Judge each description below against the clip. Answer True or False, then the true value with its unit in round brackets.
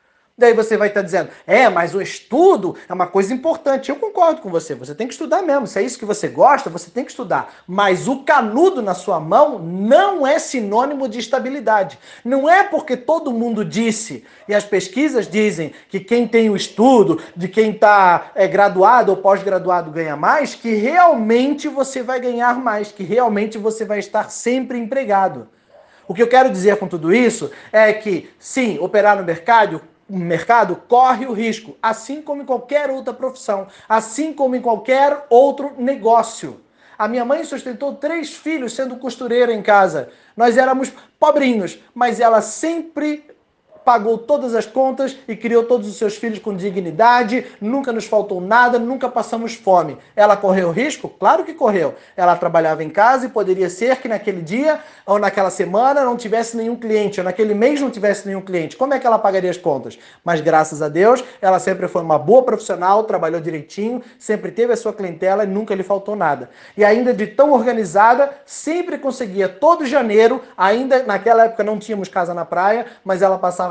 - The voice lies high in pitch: True (225 Hz)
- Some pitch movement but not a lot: True (4.8 semitones)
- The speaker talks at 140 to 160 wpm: False (185 wpm)